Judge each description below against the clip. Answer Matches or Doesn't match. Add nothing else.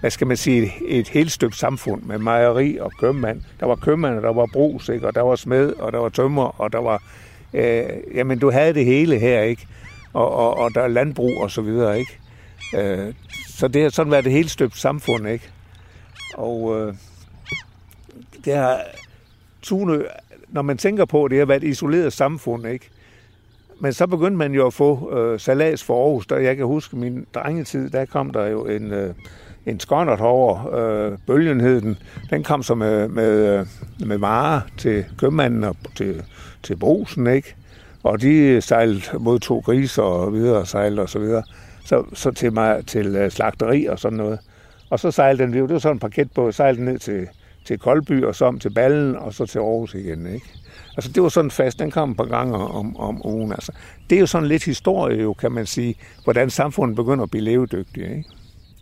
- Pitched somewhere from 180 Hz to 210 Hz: Doesn't match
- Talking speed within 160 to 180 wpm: Doesn't match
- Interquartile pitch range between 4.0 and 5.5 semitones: Matches